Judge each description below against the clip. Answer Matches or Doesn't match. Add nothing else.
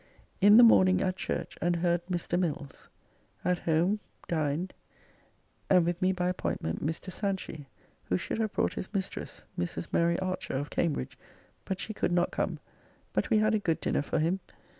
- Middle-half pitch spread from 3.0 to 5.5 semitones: Doesn't match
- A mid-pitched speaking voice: Matches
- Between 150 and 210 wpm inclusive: Matches